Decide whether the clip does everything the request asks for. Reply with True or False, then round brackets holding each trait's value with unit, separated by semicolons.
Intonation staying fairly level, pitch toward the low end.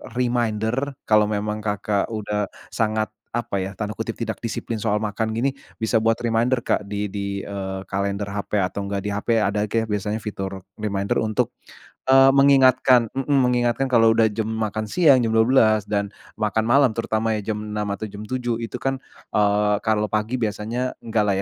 True (2.2 semitones; 110 Hz)